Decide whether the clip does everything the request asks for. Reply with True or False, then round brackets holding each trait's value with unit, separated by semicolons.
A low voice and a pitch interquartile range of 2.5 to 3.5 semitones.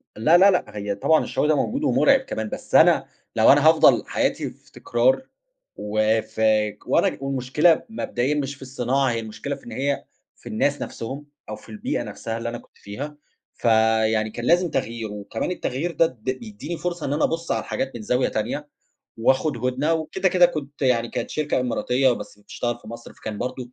False (130 Hz; 5.0 semitones)